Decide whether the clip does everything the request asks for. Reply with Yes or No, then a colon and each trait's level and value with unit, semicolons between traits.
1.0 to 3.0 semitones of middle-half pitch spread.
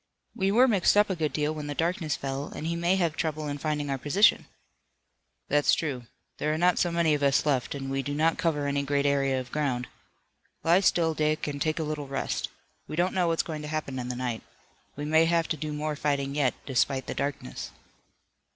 Yes: average, 2.7 semitones